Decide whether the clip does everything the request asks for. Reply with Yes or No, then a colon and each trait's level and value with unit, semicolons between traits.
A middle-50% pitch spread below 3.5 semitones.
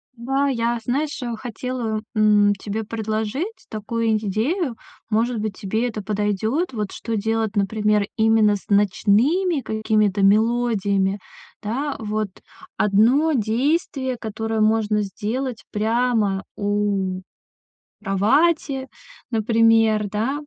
Yes: average, 2.8 semitones